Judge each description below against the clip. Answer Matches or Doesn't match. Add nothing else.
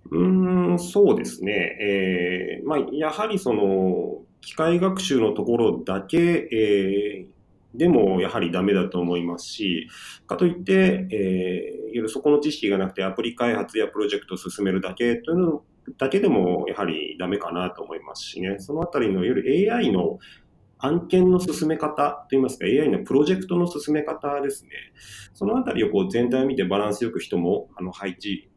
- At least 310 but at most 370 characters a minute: Matches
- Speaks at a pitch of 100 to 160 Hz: Matches